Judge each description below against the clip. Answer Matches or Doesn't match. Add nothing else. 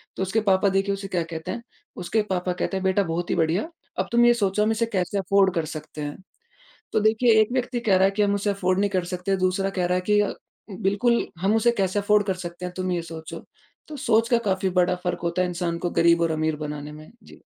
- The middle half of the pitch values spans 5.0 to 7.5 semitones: Doesn't match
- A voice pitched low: Doesn't match